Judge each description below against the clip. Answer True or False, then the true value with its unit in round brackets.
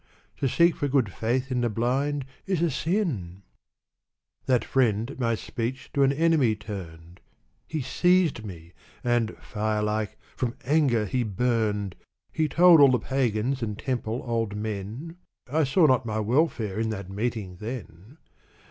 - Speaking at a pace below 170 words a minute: True (155 wpm)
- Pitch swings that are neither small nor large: True (4.5 semitones)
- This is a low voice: True (120 Hz)